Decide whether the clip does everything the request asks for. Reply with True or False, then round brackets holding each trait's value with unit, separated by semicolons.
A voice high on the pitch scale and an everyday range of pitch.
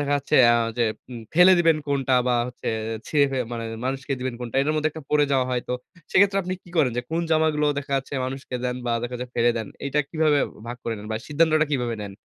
False (135 Hz; 3.8 semitones)